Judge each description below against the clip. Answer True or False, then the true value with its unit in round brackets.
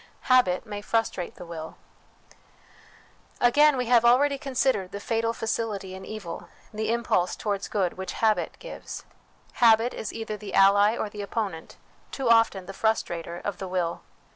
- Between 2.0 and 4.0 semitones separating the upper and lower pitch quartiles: True (3.5 semitones)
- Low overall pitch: False (215 Hz)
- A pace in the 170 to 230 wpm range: False (155 wpm)